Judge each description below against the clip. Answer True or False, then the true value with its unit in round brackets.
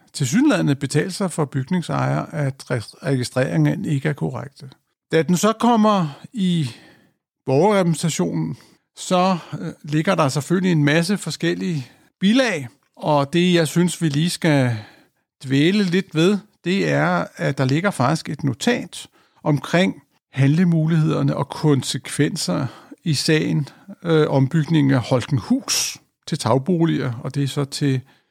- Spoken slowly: True (125 wpm)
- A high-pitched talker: False (155 Hz)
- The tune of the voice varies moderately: True (4.4 semitones)